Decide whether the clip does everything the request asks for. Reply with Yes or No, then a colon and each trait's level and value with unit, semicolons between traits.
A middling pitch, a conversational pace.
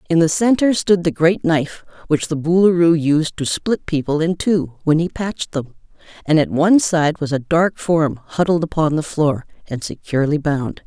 Yes: medium, 160 Hz; average, 195 wpm